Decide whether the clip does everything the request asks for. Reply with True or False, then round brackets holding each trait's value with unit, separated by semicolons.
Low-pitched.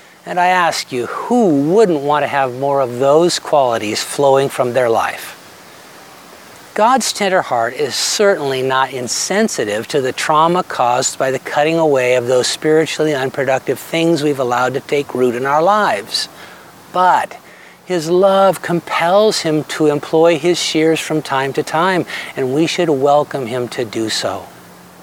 False (150 Hz)